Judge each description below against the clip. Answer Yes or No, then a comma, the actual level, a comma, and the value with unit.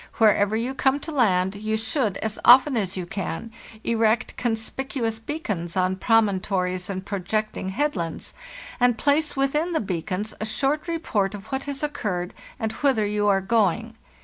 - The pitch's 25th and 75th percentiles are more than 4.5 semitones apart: Yes, wide, 5.4 semitones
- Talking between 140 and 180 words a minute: Yes, average, 165 wpm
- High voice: Yes, high, 220 Hz